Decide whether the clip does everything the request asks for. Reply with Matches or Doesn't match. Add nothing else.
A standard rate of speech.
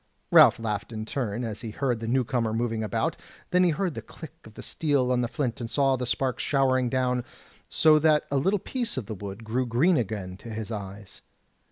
Doesn't match